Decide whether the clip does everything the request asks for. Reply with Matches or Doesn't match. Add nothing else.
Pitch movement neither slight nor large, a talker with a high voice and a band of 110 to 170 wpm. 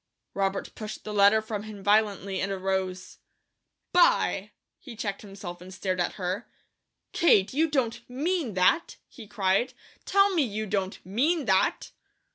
Matches